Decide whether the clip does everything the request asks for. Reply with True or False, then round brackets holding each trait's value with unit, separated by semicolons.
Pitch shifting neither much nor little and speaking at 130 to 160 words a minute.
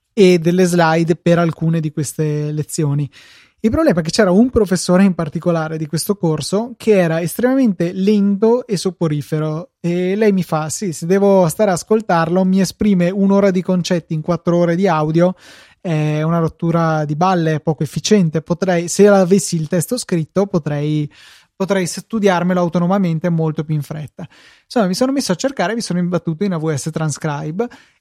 False (3.5 semitones; 170 wpm)